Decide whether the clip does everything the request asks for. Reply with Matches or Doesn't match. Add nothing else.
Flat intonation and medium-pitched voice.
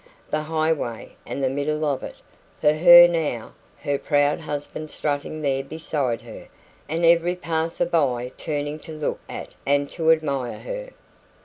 Matches